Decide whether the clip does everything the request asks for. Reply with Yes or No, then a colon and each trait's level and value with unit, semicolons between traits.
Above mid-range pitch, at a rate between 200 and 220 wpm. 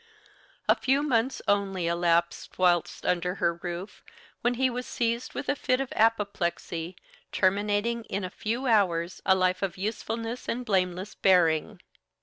No: high, 200 Hz; average, 145 wpm